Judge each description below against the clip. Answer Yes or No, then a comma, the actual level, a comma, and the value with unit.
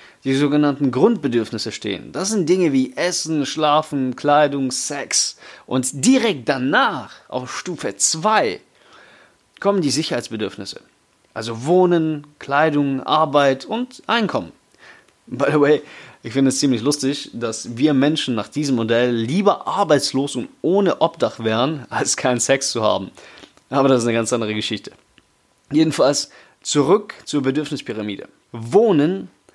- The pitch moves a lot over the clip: No, average, 4.0 semitones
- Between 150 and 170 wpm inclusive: No, average, 130 wpm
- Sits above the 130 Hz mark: Yes, medium, 140 Hz